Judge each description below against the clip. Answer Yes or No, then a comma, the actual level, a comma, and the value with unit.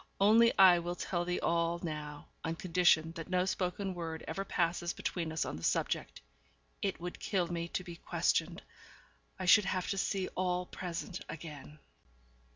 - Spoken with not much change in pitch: Yes, narrow, 1.9 semitones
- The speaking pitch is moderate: Yes, medium, 175 Hz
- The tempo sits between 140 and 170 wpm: Yes, average, 165 wpm